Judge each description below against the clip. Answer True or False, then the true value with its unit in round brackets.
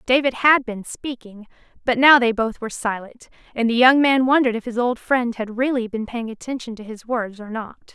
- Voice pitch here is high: True (240 Hz)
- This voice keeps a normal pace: False (220 wpm)